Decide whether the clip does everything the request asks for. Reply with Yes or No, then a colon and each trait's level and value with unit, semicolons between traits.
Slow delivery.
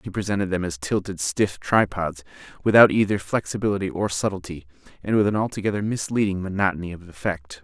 No: average, 155 wpm